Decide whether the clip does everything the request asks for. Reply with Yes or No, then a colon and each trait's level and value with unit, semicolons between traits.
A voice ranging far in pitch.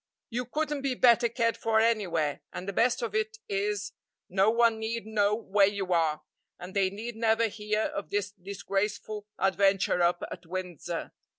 No: average, 2.9 semitones